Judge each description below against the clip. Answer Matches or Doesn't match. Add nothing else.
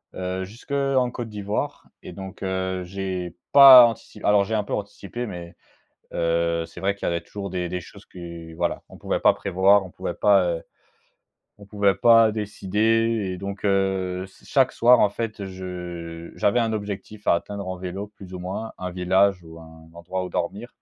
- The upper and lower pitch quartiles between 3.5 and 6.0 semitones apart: Doesn't match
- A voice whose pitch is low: Matches